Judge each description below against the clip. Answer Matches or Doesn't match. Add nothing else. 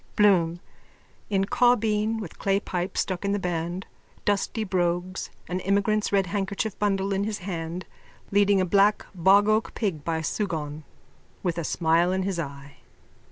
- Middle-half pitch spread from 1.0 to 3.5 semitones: Matches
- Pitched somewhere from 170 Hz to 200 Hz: Matches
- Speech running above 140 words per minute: Matches